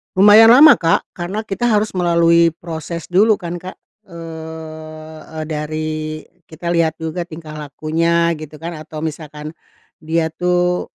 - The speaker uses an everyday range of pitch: No, narrow, 2.1 semitones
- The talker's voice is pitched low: No, medium, 165 Hz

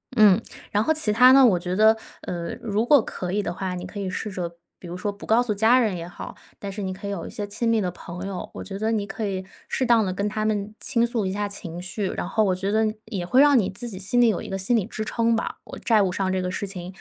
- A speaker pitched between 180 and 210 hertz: Yes, high, 205 Hz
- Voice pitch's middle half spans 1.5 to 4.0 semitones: Yes, average, 2.9 semitones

